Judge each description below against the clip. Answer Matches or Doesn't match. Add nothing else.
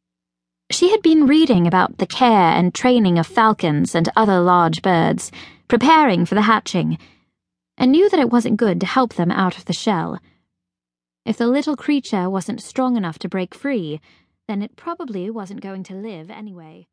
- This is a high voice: Matches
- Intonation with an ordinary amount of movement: Doesn't match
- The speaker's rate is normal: Matches